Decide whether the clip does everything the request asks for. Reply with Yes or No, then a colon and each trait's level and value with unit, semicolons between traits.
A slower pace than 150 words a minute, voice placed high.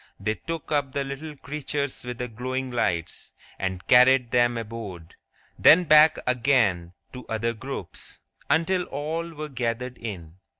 No: average, 140 wpm; low, 125 Hz